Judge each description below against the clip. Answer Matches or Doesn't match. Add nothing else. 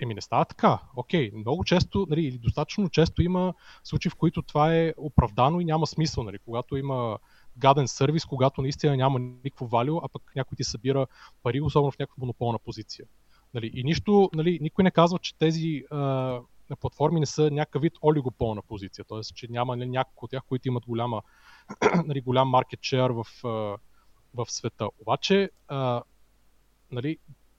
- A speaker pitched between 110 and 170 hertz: Matches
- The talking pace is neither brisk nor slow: Doesn't match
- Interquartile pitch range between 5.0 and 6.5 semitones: Doesn't match